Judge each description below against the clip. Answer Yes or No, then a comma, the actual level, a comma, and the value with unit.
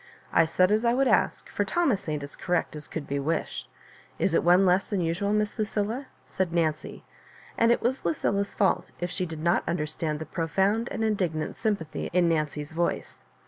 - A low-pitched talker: No, medium, 180 Hz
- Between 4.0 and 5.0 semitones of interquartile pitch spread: Yes, average, 4.6 semitones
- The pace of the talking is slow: No, average, 195 wpm